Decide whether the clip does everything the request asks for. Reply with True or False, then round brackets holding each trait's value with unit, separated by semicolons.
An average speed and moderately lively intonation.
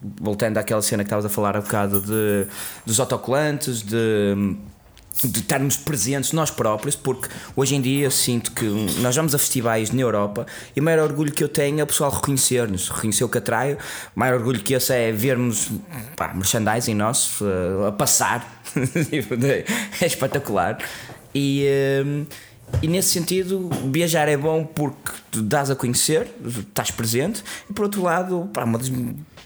True (170 wpm; 4.9 semitones)